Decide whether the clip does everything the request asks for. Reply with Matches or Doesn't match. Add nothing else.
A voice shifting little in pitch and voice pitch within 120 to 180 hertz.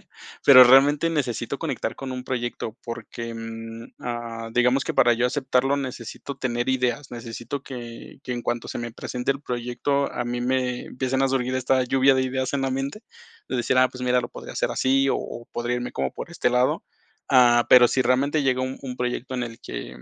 Matches